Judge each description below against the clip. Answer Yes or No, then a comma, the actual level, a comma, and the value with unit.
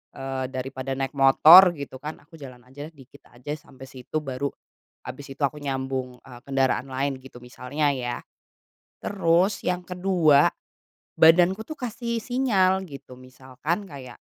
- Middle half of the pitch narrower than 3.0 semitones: No, average, 4.9 semitones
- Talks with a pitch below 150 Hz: Yes, medium, 140 Hz